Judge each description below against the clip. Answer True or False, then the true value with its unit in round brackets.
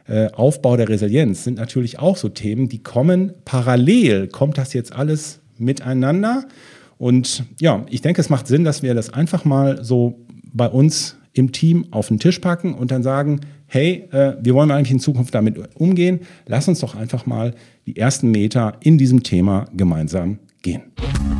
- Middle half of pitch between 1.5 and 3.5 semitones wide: False (4.4 semitones)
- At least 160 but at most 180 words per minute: True (170 wpm)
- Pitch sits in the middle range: False (130 Hz)